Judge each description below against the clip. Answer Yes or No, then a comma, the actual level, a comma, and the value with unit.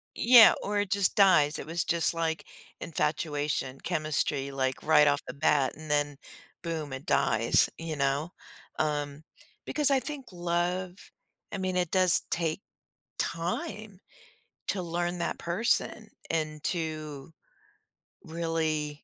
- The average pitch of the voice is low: No, medium, 160 Hz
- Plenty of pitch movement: No, average, 3.2 semitones